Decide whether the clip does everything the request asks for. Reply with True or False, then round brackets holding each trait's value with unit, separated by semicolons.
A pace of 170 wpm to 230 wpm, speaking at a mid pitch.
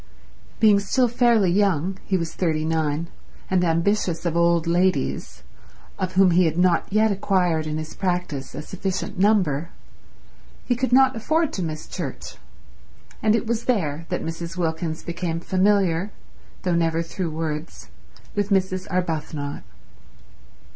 False (135 wpm; 180 Hz)